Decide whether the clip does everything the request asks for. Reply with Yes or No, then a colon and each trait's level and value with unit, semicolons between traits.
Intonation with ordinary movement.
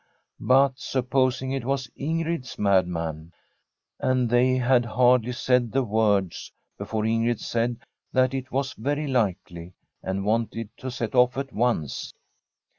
Yes: average, 3.2 semitones